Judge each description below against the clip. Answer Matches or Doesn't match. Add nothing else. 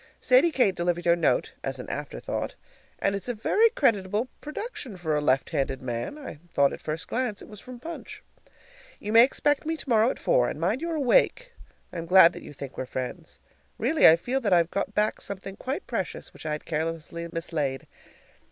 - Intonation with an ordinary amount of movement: Doesn't match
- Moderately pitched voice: Doesn't match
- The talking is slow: Doesn't match